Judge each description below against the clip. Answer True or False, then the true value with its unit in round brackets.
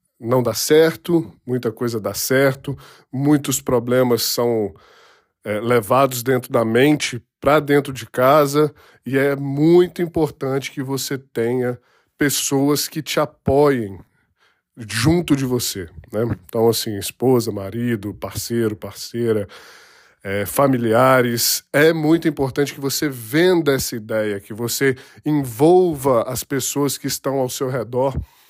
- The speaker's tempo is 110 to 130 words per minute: True (125 wpm)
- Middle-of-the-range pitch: False (130 Hz)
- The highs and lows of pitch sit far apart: False (3.8 semitones)